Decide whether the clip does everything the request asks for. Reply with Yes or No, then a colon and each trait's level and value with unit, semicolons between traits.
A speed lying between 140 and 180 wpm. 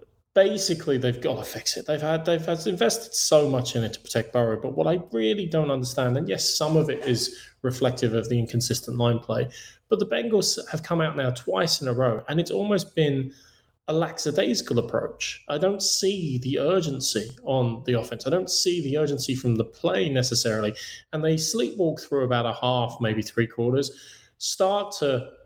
No: average, 195 wpm